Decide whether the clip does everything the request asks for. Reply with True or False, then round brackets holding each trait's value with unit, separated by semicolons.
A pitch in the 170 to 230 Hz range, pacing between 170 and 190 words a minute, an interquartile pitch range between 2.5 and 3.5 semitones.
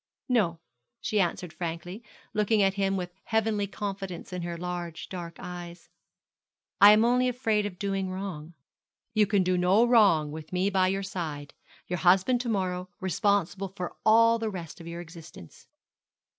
False (190 Hz; 160 wpm; 3.0 semitones)